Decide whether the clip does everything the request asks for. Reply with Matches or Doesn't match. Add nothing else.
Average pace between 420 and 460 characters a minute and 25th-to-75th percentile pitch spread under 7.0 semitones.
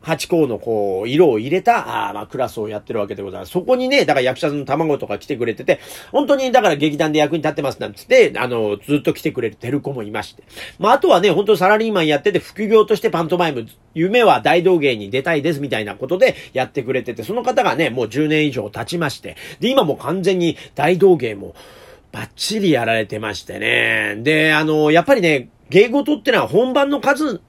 Matches